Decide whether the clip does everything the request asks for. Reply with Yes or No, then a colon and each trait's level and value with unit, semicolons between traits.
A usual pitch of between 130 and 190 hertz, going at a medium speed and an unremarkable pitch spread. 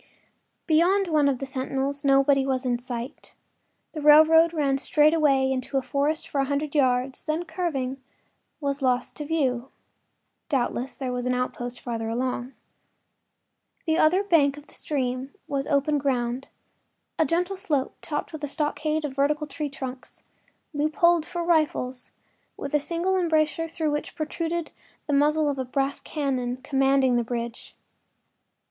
No: very high, 280 Hz; average, 150 wpm; average, 3.0 semitones